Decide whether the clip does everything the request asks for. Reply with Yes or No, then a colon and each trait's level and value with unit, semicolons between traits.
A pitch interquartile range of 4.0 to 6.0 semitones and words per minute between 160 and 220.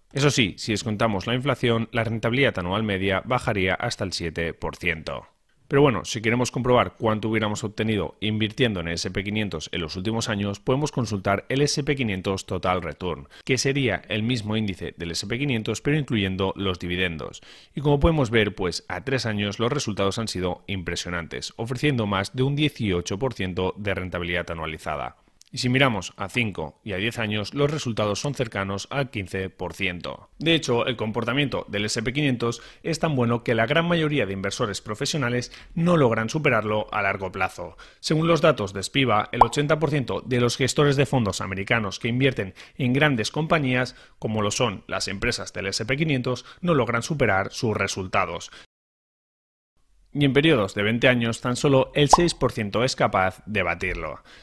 Yes: average, 5.2 semitones; average, 165 wpm